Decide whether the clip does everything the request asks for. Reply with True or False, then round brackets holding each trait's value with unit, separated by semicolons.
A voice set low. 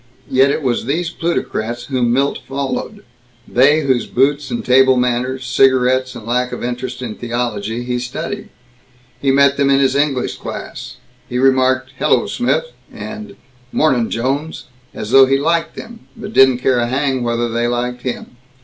True (130 Hz)